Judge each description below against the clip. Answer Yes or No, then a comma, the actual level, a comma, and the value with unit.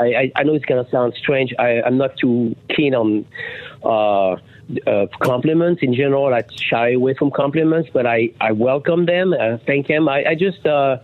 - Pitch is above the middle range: No, low, 130 Hz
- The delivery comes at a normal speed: Yes, average, 190 wpm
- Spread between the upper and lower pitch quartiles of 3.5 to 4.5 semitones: Yes, average, 4.2 semitones